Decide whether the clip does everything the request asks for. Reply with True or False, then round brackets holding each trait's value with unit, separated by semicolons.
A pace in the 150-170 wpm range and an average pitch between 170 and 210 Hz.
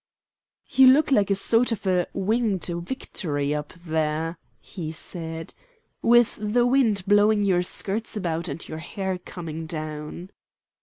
False (140 wpm; 185 Hz)